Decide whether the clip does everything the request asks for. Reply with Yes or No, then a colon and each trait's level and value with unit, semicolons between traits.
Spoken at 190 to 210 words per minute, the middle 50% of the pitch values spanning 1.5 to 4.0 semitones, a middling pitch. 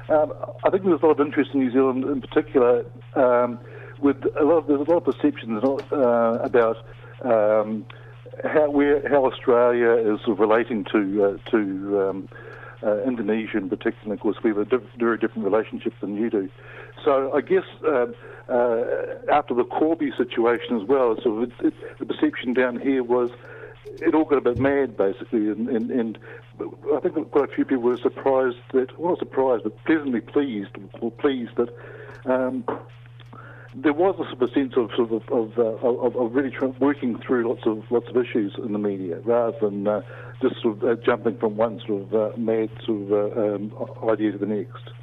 No: fast, 205 wpm; average, 3.6 semitones; low, 120 Hz